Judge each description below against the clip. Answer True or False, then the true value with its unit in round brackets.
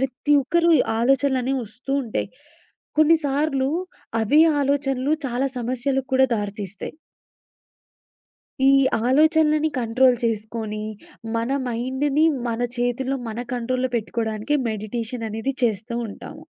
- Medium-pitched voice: False (255 Hz)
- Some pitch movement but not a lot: True (3.3 semitones)